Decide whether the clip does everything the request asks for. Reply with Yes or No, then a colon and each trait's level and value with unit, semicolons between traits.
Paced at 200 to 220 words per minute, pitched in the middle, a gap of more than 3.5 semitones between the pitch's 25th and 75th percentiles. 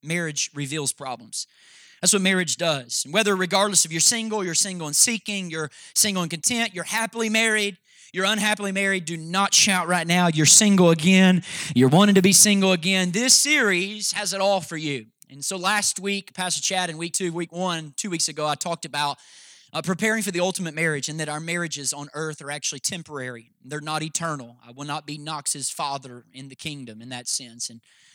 Yes: fast, 205 wpm; medium, 170 Hz; average, 4.8 semitones